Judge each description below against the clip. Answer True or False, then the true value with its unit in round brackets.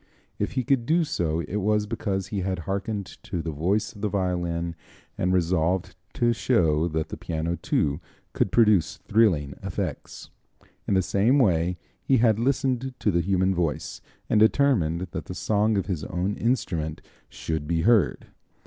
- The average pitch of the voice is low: True (95 Hz)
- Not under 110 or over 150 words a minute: False (165 wpm)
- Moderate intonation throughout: True (4.5 semitones)